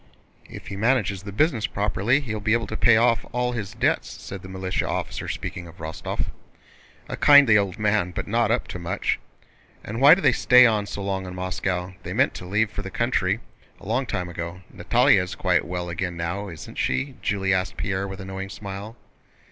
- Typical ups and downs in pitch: Yes, average, 3.4 semitones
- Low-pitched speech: Yes, low, 100 Hz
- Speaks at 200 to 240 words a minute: Yes, fast, 205 wpm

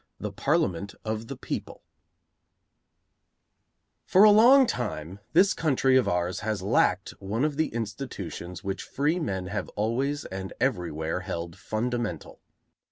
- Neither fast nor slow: No, slow, 130 wpm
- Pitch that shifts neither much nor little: No, wide, 6.9 semitones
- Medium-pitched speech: No, low, 110 Hz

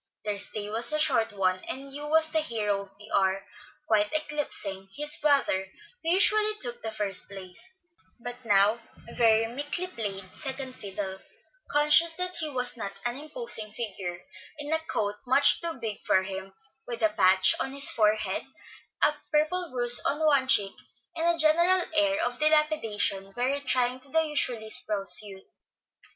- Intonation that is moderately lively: No, wide, 6.7 semitones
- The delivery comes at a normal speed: Yes, average, 165 wpm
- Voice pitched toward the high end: Yes, high, 245 Hz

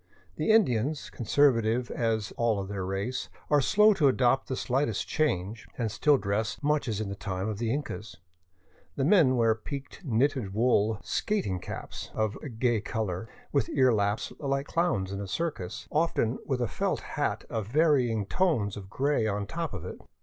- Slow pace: No, average, 175 wpm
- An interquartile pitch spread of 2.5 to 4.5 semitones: No, wide, 5.5 semitones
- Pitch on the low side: Yes, low, 115 Hz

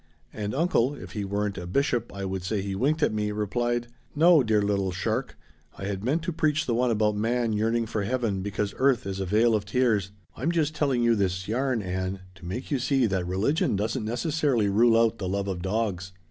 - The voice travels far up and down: No, average, 4.1 semitones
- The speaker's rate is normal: No, fast, 215 wpm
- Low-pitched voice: Yes, low, 110 Hz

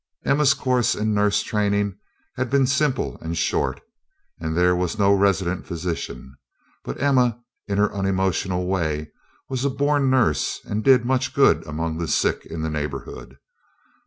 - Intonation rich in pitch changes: Yes, wide, 7.1 semitones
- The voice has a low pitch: Yes, low, 100 Hz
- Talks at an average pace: Yes, average, 155 wpm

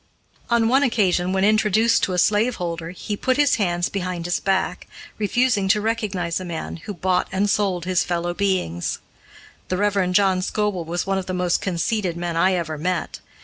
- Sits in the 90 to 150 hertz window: No, medium, 185 Hz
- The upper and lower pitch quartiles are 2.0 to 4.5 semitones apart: Yes, average, 2.9 semitones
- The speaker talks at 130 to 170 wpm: No, average, 185 wpm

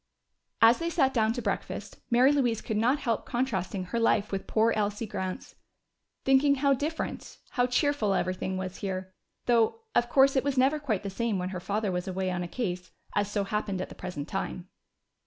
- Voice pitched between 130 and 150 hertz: No, high, 220 Hz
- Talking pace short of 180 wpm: No, average, 195 wpm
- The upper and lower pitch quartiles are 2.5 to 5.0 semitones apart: No, wide, 5.6 semitones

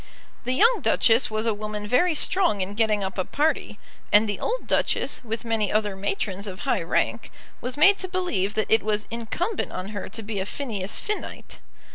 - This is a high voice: Yes, high, 220 Hz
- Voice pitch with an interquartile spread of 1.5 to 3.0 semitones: No, average, 4.0 semitones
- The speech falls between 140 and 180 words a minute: No, average, 195 wpm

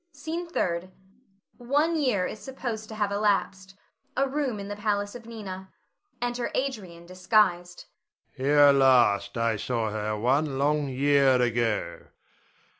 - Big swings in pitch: Yes, wide, 8.8 semitones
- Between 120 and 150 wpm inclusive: Yes, slow, 135 wpm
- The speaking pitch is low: No, medium, 185 Hz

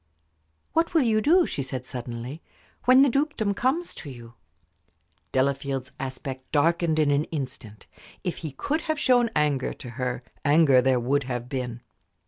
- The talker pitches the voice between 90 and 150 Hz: Yes, medium, 140 Hz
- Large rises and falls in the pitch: Yes, wide, 9.0 semitones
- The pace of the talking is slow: No, average, 155 wpm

